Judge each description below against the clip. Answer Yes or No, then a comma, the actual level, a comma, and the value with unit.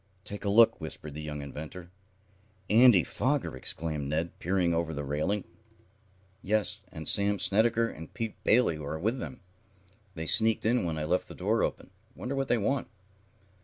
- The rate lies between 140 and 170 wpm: Yes, average, 165 wpm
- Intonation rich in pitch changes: Yes, wide, 6.0 semitones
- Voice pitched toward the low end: Yes, very low, 90 Hz